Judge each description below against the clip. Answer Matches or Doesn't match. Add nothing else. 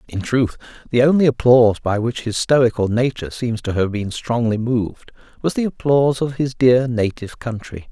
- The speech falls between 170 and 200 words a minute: Matches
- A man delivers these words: Matches